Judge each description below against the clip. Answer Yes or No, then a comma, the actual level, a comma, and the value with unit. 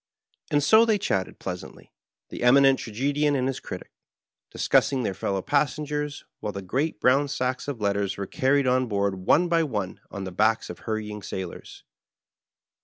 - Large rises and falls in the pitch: Yes, wide, 6.1 semitones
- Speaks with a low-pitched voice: Yes, low, 125 Hz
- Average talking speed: Yes, average, 170 wpm